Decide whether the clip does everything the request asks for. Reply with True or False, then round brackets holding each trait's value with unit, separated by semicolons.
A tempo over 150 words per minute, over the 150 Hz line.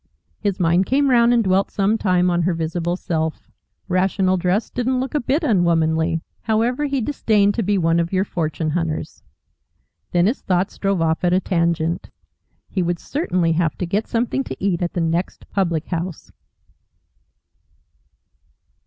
True (160 wpm; 185 Hz)